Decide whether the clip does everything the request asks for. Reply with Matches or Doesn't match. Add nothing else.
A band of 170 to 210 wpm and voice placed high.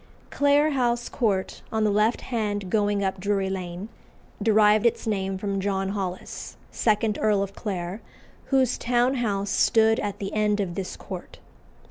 Doesn't match